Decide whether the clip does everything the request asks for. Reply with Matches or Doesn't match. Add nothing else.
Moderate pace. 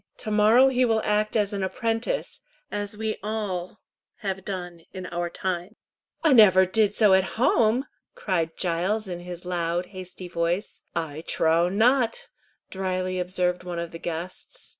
Matches